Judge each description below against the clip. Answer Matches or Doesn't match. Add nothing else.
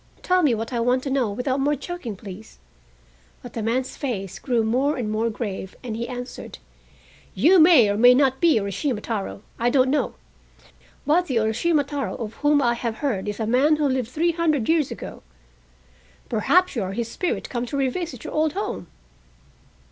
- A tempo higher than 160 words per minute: Matches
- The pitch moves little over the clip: Doesn't match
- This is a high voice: Matches